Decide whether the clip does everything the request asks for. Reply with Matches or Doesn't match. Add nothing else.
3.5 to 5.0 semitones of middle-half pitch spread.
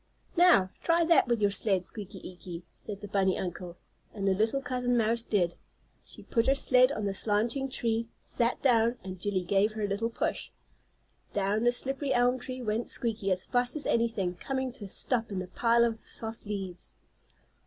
Matches